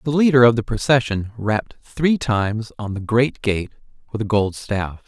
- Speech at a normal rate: Yes, average, 190 wpm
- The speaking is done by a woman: No, male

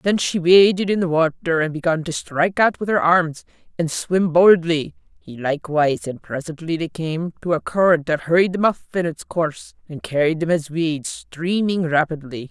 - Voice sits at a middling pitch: Yes, medium, 165 Hz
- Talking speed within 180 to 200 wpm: Yes, average, 185 wpm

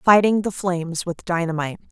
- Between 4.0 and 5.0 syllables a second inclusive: No, 5.6 syllables/s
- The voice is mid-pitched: Yes, medium, 180 Hz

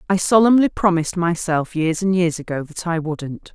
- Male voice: No, female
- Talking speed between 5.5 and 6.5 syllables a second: No, 5.0 syllables/s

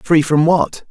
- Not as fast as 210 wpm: Yes, average, 200 wpm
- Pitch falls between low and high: Yes, medium, 160 Hz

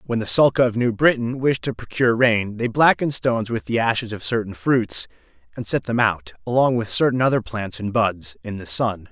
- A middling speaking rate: No, fast, 215 wpm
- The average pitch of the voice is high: No, low, 110 Hz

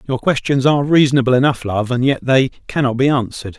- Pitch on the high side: No, low, 130 Hz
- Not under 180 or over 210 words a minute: Yes, average, 200 wpm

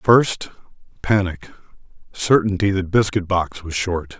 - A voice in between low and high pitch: No, low, 100 Hz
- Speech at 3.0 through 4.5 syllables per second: Yes, 4.0 syllables/s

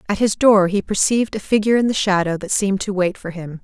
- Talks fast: Yes, fast, 265 wpm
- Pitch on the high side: Yes, high, 200 Hz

